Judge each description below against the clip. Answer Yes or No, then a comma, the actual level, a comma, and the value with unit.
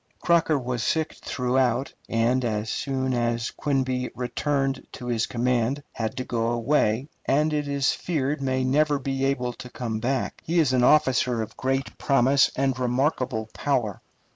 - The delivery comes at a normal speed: Yes, average, 160 wpm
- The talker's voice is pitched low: Yes, low, 130 Hz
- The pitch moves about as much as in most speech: No, narrow, 2.3 semitones